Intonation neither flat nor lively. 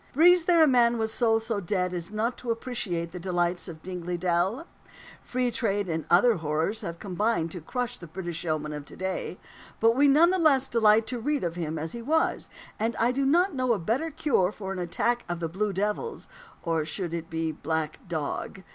No: wide, 6.2 semitones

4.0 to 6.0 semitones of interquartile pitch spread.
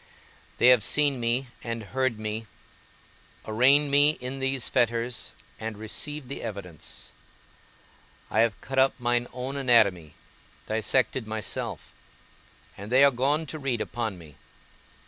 No: average, 3.5 semitones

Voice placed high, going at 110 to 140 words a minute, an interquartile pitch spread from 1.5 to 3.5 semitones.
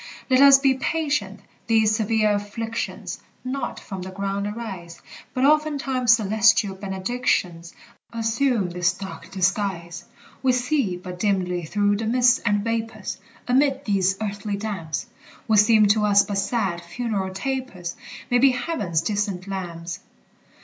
No: high, 210 Hz; slow, 135 wpm; average, 4.1 semitones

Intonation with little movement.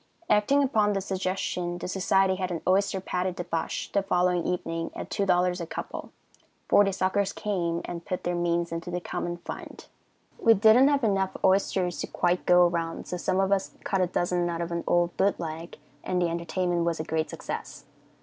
Yes: narrow, 2.1 semitones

